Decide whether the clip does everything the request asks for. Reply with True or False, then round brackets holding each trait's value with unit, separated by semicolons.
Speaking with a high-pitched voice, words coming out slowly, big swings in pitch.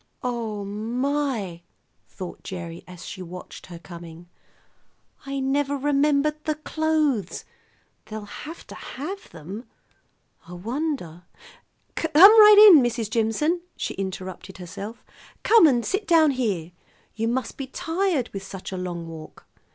True (235 Hz; 130 wpm; 8.3 semitones)